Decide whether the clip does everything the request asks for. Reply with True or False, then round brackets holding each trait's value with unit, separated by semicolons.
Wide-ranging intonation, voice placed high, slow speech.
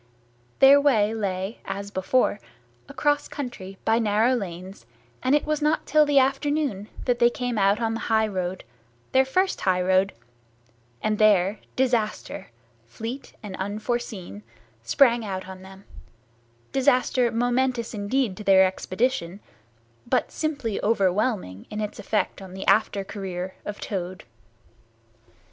False (4.9 semitones; 215 Hz; 130 wpm)